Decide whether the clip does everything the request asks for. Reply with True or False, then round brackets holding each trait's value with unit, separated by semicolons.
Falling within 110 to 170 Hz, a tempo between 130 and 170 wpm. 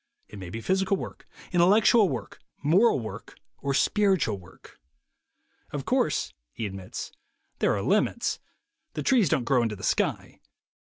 True (140 Hz; 145 wpm)